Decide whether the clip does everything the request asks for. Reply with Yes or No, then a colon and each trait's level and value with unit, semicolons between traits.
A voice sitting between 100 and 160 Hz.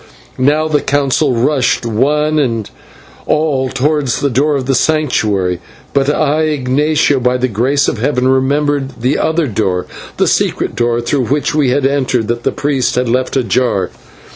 Yes: low, 135 Hz